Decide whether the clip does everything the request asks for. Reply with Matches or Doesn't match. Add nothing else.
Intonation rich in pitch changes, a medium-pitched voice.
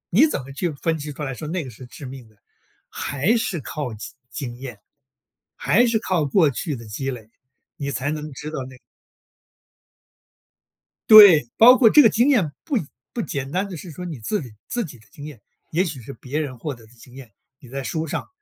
Matches